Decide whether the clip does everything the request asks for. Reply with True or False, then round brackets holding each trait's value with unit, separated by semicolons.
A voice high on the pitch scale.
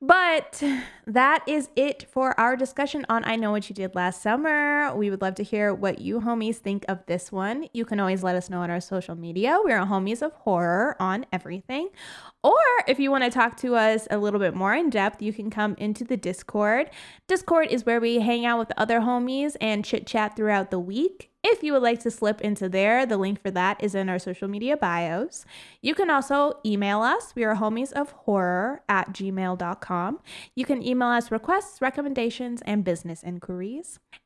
True (225 Hz)